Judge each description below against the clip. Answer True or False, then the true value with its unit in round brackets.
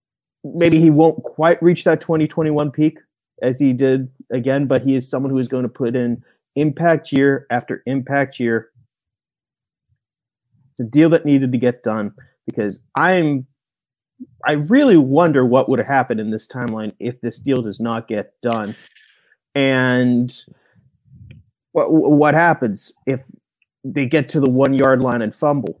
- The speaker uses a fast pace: False (160 wpm)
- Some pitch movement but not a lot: True (3.4 semitones)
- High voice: False (130 Hz)